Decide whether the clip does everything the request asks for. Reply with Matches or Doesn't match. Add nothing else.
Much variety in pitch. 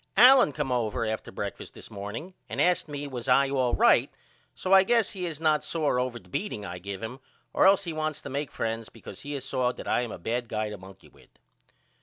Matches